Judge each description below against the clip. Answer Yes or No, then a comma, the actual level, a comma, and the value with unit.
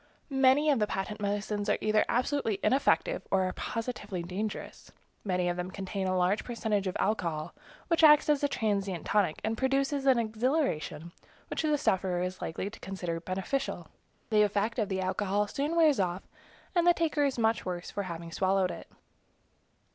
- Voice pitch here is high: Yes, high, 210 Hz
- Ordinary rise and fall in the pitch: No, wide, 6.1 semitones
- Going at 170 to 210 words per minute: Yes, average, 175 wpm